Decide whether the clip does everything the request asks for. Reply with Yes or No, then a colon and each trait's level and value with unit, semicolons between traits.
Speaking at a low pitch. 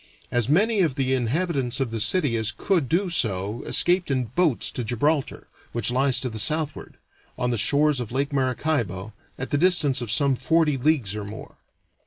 Yes: low, 130 Hz